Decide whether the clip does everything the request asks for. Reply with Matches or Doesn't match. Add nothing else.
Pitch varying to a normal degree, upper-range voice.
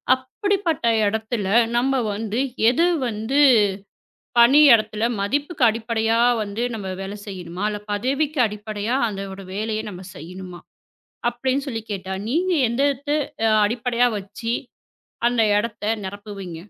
Matches